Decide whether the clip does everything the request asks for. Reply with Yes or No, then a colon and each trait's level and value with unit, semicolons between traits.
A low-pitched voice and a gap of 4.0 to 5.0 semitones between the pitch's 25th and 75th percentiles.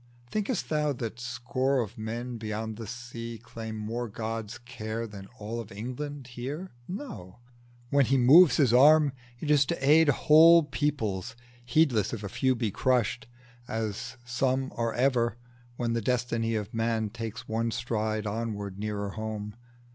No: low, 115 Hz; average, 3.2 semitones